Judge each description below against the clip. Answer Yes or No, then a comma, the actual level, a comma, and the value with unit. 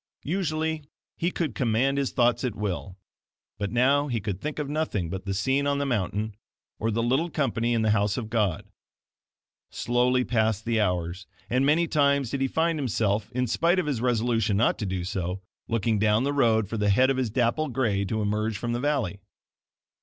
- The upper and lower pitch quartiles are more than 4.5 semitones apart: Yes, average, 4.9 semitones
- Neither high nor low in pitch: No, low, 115 Hz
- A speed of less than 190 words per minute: No, average, 200 wpm